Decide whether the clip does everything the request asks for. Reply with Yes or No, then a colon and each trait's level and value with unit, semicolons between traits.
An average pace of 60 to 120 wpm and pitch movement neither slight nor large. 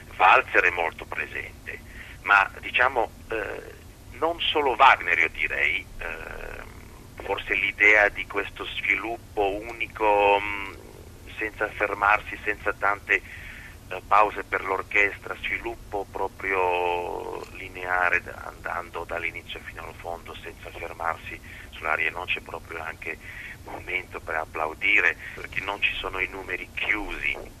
Yes: slow, 115 wpm; average, 3.0 semitones